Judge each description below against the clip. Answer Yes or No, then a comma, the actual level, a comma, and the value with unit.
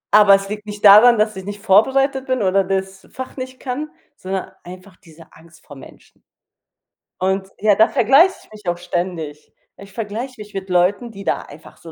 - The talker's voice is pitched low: No, high, 200 Hz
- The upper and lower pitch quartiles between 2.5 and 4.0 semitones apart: Yes, average, 3.4 semitones